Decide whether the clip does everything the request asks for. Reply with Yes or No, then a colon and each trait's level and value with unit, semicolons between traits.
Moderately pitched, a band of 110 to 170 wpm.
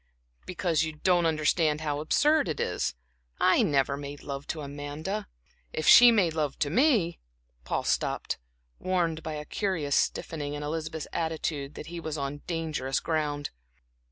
Yes: medium, 155 Hz; average, 155 wpm